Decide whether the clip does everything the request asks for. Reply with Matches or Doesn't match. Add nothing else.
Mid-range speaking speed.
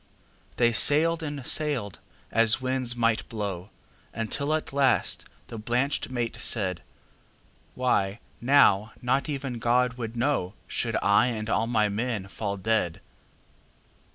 Doesn't match